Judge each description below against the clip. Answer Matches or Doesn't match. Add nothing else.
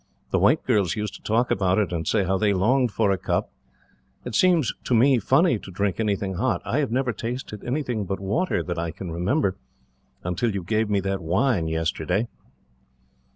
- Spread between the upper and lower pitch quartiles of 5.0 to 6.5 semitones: Doesn't match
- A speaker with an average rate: Matches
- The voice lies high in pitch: Doesn't match